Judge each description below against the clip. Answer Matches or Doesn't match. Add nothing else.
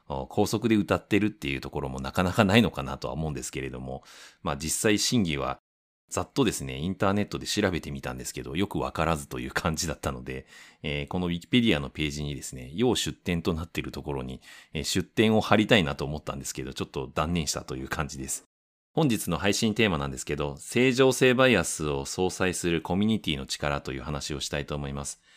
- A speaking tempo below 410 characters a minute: Doesn't match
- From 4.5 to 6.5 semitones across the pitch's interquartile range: Matches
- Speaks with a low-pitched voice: Matches